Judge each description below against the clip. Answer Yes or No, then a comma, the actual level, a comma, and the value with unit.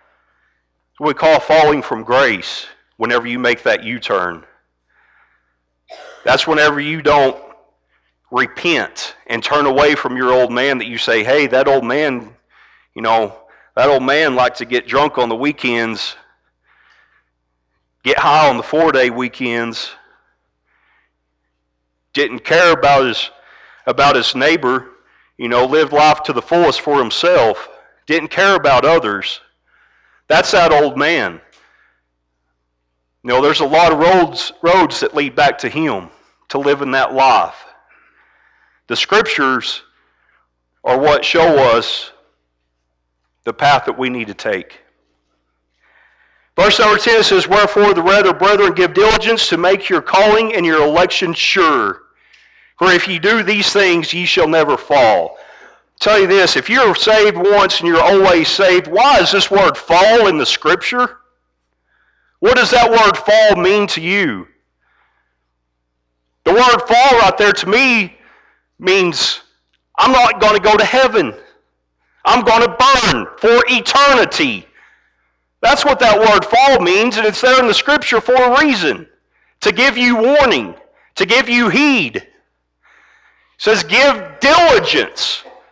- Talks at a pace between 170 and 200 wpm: No, average, 145 wpm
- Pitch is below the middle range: No, medium, 170 Hz